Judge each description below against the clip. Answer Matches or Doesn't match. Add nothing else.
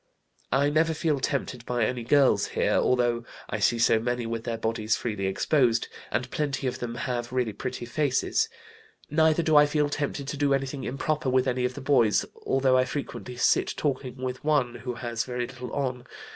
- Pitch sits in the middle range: Doesn't match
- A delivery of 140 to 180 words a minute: Doesn't match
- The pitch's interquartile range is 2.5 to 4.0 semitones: Matches